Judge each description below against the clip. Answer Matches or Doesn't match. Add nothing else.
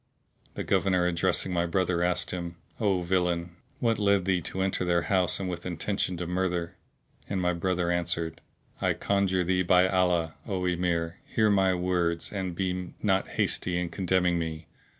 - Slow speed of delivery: Doesn't match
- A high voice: Doesn't match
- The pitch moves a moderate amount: Doesn't match